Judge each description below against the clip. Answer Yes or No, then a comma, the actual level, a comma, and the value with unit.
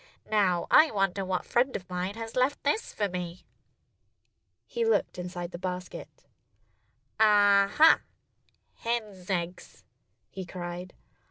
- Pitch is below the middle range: No, high, 195 Hz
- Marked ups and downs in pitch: No, average, 3.6 semitones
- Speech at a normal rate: No, slow, 120 wpm